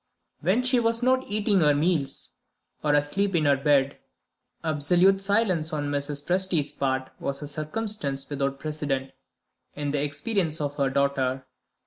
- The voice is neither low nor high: Yes, medium, 150 Hz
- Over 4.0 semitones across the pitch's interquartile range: Yes, average, 5.3 semitones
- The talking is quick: No, average, 145 wpm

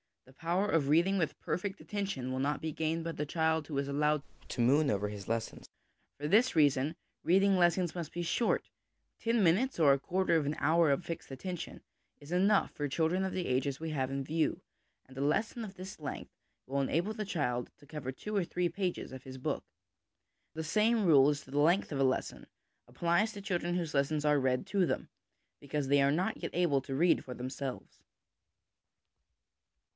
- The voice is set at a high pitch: No, medium, 160 Hz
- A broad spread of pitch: No, average, 4.6 semitones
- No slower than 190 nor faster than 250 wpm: Yes, average, 200 wpm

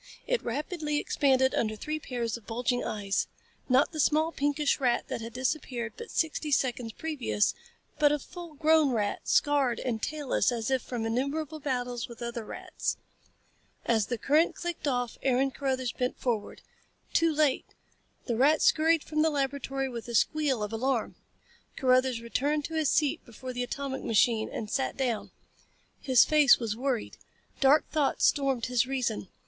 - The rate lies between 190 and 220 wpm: No, average, 165 wpm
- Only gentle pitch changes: No, average, 3.9 semitones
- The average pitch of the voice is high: Yes, very high, 265 Hz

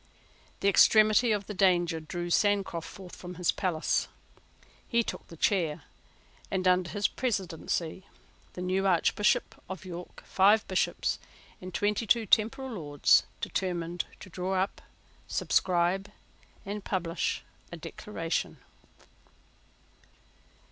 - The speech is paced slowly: Yes, slow, 115 wpm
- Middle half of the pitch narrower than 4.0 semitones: Yes, average, 2.8 semitones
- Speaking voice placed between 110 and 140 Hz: No, medium, 185 Hz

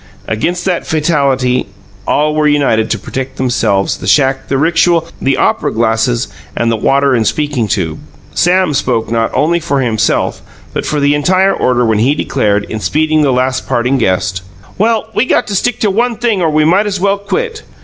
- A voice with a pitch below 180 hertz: Yes, medium, 140 Hz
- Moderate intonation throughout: No, wide, 6.6 semitones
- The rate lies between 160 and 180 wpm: No, average, 190 wpm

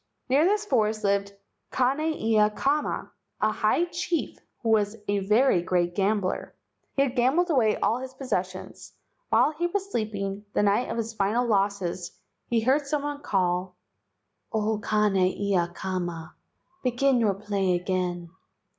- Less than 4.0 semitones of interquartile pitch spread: No, average, 5.2 semitones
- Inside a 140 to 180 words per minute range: Yes, average, 145 wpm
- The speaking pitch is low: No, high, 215 Hz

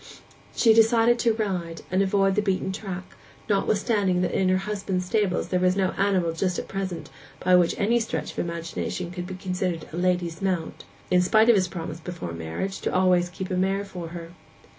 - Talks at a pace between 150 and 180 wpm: No, average, 195 wpm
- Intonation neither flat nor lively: No, narrow, 2.0 semitones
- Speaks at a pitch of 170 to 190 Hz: Yes, medium, 185 Hz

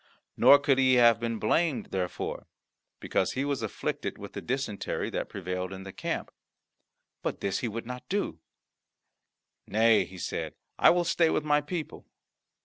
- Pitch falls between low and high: No, low, 120 Hz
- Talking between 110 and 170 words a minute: Yes, average, 160 wpm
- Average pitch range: No, wide, 6.2 semitones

